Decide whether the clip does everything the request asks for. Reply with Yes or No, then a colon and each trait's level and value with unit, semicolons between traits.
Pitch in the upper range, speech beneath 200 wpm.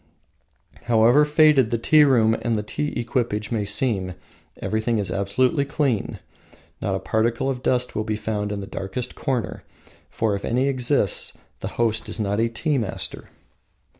No: low, 115 Hz; average, 165 wpm